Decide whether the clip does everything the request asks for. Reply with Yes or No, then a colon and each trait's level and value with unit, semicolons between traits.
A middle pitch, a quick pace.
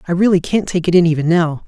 Yes: medium, 175 Hz; fast, 285 wpm